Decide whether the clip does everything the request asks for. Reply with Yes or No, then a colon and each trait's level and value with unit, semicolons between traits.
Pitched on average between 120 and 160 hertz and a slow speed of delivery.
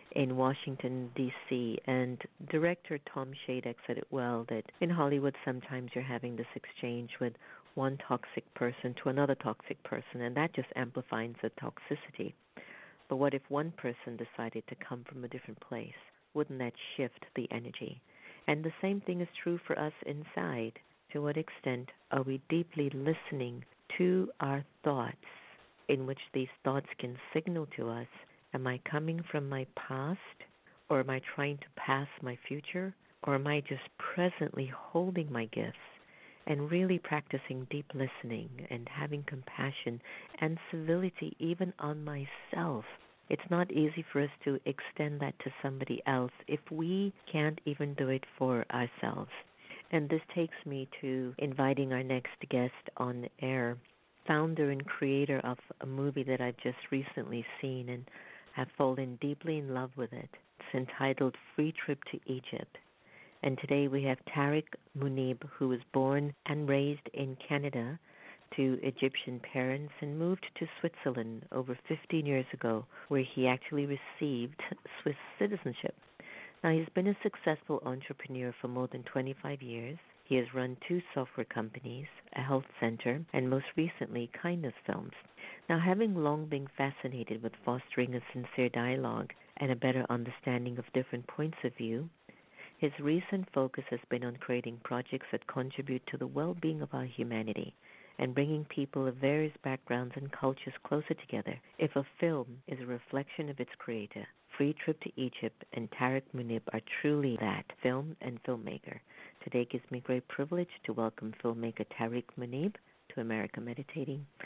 No: low, 135 Hz; average, 160 wpm